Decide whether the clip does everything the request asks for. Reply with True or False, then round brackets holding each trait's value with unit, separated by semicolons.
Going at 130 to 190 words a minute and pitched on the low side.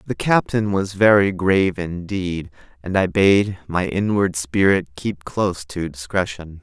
True (145 wpm; 90 Hz)